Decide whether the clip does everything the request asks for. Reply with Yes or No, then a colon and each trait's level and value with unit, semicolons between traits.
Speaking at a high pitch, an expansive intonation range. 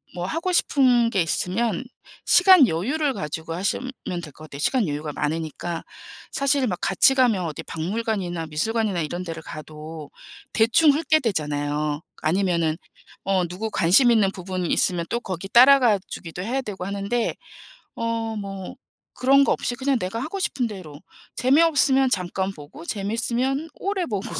Yes: high, 200 Hz; wide, 7.0 semitones